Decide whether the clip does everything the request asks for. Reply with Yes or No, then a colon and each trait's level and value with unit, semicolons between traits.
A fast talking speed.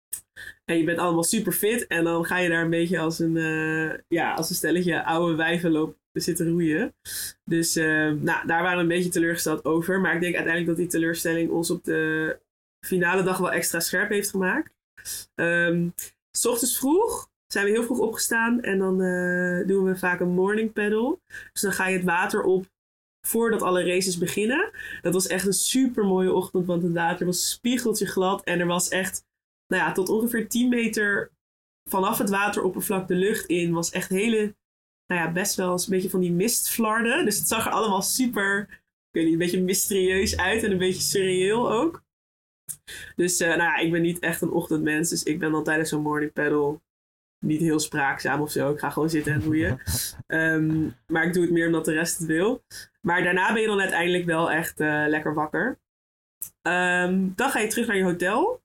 Yes: fast, 205 wpm